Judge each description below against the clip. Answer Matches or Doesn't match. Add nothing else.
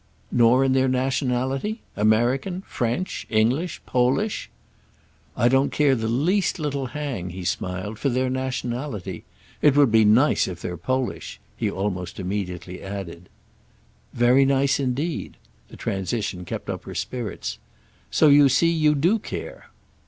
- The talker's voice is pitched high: Doesn't match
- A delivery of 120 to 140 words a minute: Matches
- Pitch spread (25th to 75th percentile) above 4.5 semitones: Matches